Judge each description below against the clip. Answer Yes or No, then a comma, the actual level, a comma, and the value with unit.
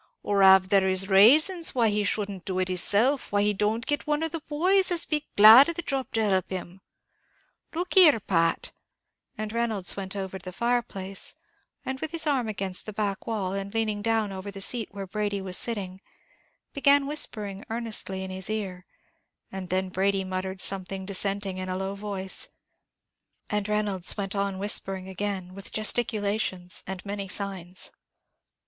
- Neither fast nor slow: Yes, average, 180 wpm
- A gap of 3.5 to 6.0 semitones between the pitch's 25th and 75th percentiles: No, average, 3.0 semitones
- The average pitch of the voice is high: Yes, high, 200 Hz